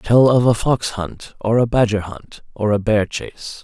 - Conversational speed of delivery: No, fast, 215 wpm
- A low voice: Yes, low, 110 Hz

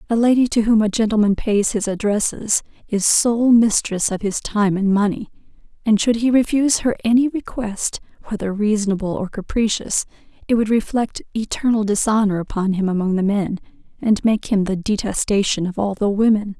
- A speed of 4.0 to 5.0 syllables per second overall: No, 5.2 syllables/s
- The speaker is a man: No, female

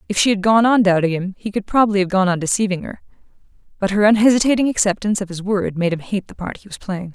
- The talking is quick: Yes, fast, 250 wpm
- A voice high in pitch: Yes, high, 200 Hz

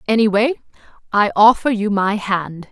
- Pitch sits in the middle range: No, high, 210 Hz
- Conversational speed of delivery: No, slow, 130 wpm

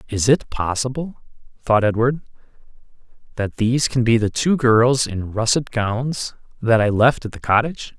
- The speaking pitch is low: Yes, low, 120 Hz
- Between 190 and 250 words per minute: No, average, 160 wpm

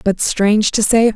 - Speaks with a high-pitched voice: Yes, high, 215 Hz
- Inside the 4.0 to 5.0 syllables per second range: Yes, 4.8 syllables/s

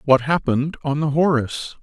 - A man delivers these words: Yes, male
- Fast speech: No, average, 165 wpm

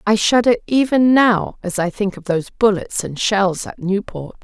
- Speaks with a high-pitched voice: Yes, high, 200 Hz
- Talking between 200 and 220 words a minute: No, average, 190 wpm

